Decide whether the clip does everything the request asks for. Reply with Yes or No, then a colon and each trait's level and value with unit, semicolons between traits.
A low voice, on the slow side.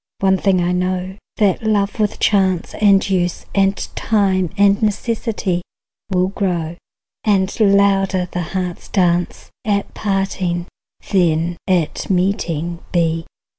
No: high, 190 Hz; slow, 120 wpm